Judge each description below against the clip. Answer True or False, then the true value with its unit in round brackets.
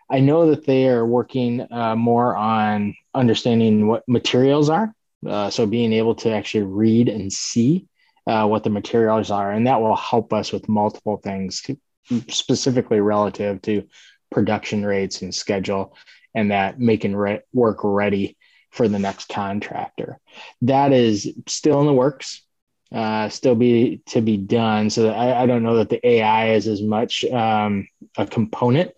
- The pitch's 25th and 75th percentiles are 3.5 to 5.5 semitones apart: False (2.8 semitones)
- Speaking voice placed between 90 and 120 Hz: True (110 Hz)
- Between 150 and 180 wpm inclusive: True (165 wpm)